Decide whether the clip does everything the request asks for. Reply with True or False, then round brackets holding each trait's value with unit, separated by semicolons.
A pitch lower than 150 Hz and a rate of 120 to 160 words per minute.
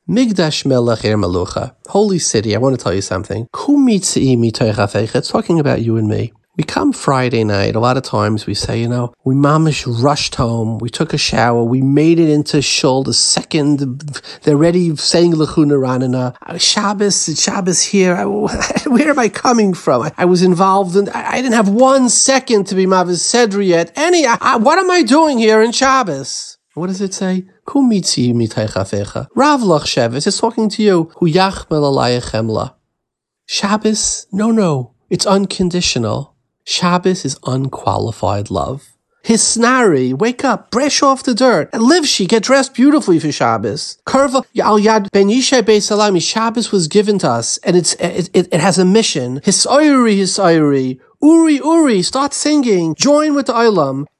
False (180 Hz; 155 wpm)